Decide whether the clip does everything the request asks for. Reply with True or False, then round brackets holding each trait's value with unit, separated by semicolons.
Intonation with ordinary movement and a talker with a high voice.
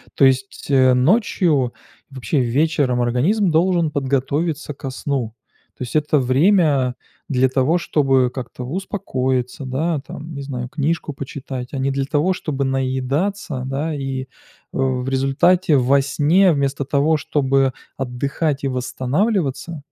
False (3.2 semitones; 140 Hz)